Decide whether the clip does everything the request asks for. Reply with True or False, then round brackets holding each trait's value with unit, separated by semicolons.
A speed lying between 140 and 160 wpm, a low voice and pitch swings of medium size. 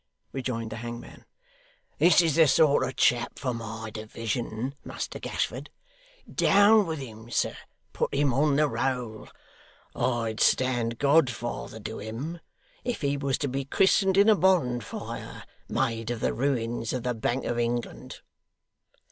True (145 wpm; 125 Hz; 3.8 semitones)